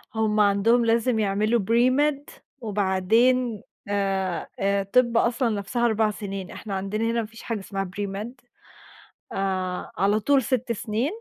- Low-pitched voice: No, high, 215 Hz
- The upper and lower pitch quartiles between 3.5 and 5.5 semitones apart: No, average, 3.1 semitones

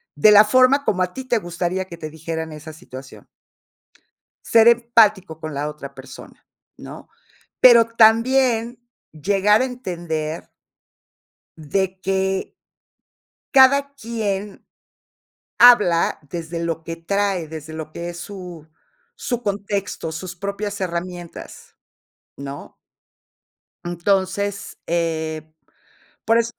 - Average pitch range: Yes, average, 5.0 semitones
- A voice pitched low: No, high, 190 Hz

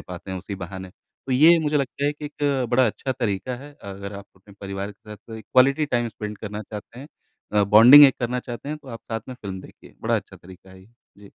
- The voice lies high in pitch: No, low, 115 Hz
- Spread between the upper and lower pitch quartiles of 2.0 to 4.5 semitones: No, average, 5.0 semitones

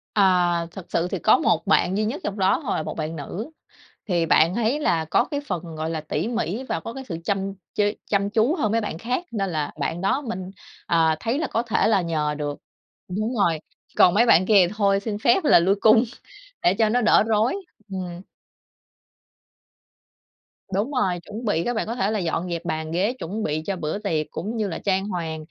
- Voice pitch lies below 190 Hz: No, high, 195 Hz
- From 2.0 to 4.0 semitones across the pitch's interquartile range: No, average, 4.8 semitones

